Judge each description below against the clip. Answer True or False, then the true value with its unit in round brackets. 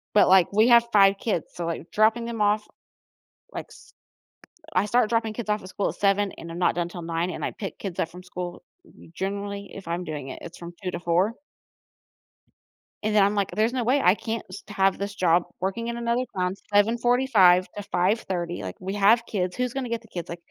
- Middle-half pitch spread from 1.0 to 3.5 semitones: False (3.9 semitones)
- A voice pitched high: True (200 Hz)